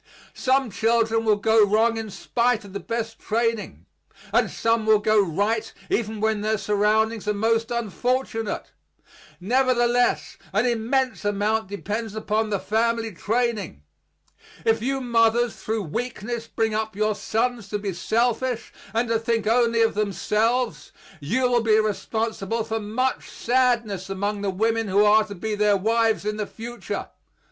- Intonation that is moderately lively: No, narrow, 1.9 semitones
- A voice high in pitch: Yes, high, 220 Hz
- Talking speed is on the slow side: No, average, 150 wpm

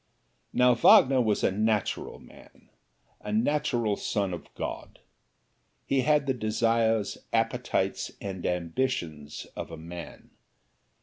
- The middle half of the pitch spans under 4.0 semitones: No, average, 4.7 semitones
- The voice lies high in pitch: No, low, 110 Hz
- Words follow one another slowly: Yes, slow, 115 wpm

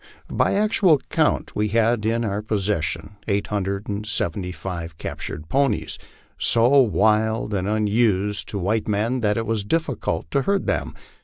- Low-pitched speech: Yes, low, 105 Hz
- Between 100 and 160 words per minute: Yes, average, 155 wpm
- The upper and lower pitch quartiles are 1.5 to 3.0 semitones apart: Yes, average, 2.7 semitones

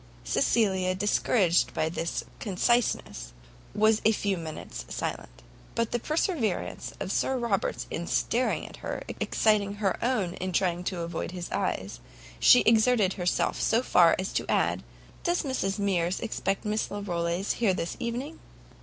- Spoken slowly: No, average, 145 wpm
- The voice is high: Yes, high, 200 Hz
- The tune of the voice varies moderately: Yes, average, 4.5 semitones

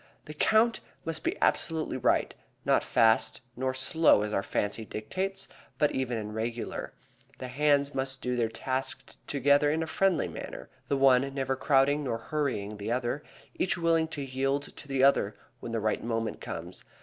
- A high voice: No, low, 135 Hz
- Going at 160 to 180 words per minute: Yes, average, 175 wpm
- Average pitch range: Yes, average, 4.3 semitones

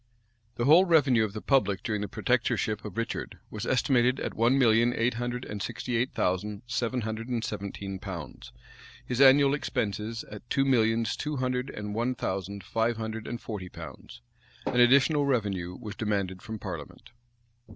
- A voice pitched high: No, low, 115 Hz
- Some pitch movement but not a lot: Yes, average, 3.5 semitones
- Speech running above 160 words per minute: Yes, average, 170 wpm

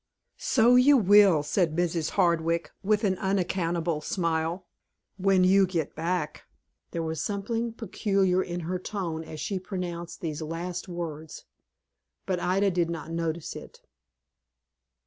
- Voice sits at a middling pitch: Yes, medium, 175 Hz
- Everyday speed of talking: No, slow, 130 wpm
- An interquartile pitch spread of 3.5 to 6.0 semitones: No, average, 2.9 semitones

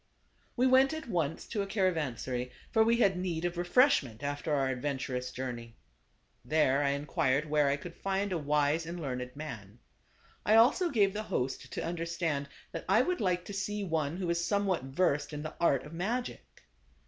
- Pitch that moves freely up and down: Yes, wide, 5.8 semitones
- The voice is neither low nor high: Yes, medium, 165 Hz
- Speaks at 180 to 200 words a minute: Yes, average, 195 wpm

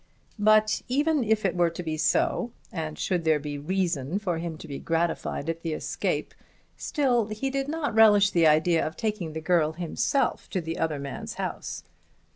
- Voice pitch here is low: No, medium, 175 Hz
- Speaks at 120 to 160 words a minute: No, average, 180 wpm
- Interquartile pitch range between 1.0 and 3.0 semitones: No, wide, 5.4 semitones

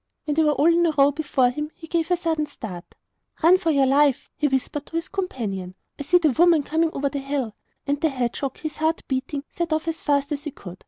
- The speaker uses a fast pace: Yes, fast, 245 wpm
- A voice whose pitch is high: Yes, very high, 295 Hz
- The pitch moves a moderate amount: Yes, average, 3.1 semitones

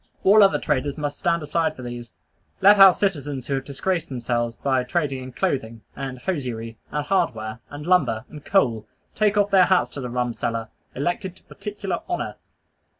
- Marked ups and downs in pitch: Yes, wide, 6.9 semitones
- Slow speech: No, average, 180 wpm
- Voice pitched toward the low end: No, medium, 145 Hz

